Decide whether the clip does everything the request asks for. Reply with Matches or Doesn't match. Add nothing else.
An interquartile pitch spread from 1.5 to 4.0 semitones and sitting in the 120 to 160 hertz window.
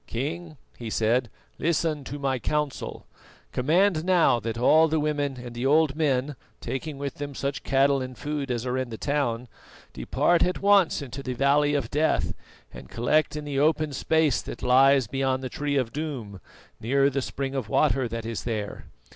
Matches